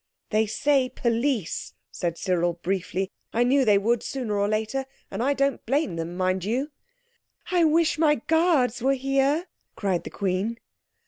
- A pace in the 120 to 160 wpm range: Yes, average, 155 wpm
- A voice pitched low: No, high, 235 Hz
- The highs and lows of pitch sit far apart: Yes, wide, 6.0 semitones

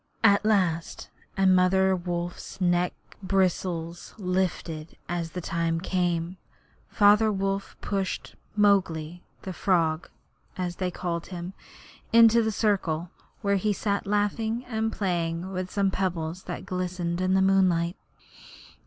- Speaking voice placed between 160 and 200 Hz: Yes, medium, 185 Hz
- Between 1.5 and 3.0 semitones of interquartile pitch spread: Yes, narrow, 2.4 semitones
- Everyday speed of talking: No, slow, 125 wpm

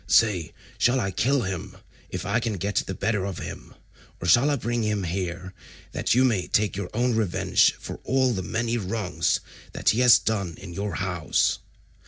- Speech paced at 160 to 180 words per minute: No, average, 190 wpm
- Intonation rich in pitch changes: No, average, 4.2 semitones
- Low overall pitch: Yes, low, 105 Hz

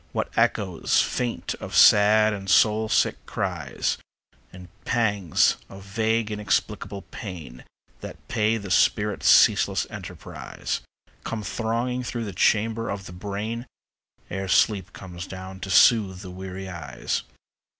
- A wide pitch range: No, average, 2.9 semitones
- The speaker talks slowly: Yes, slow, 130 wpm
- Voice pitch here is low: Yes, low, 100 Hz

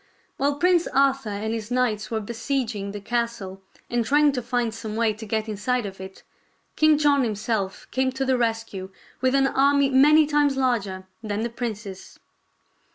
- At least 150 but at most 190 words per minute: Yes, average, 175 wpm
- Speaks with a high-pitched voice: Yes, high, 235 Hz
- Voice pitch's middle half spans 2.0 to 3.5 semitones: No, average, 4.1 semitones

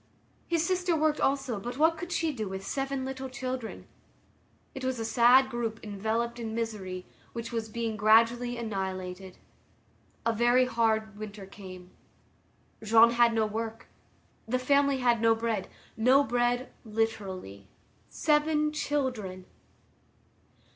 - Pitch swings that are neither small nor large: Yes, average, 3.4 semitones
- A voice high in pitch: Yes, high, 230 Hz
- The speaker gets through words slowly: Yes, slow, 130 wpm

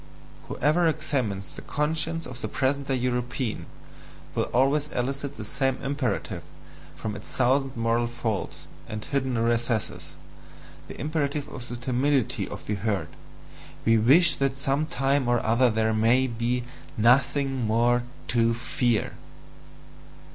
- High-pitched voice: No, low, 125 Hz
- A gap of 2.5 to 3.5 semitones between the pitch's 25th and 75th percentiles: Yes, average, 3.1 semitones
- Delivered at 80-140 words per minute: Yes, slow, 135 wpm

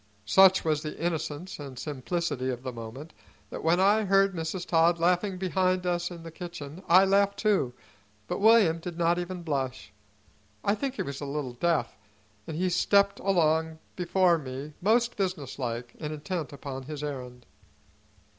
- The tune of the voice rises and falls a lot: No, average, 4.5 semitones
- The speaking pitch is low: No, medium, 165 Hz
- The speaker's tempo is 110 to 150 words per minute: No, average, 165 wpm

